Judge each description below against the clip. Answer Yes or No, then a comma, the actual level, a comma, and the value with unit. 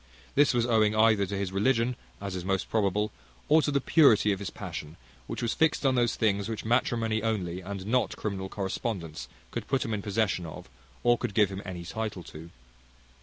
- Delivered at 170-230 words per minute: Yes, average, 200 wpm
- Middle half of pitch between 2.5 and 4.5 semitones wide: Yes, average, 3.3 semitones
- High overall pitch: No, low, 105 Hz